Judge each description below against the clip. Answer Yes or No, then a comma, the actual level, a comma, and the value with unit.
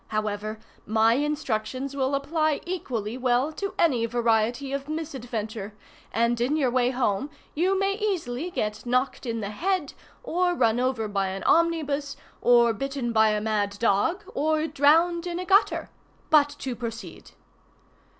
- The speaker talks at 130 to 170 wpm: Yes, average, 150 wpm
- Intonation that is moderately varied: No, wide, 5.8 semitones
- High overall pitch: Yes, very high, 255 Hz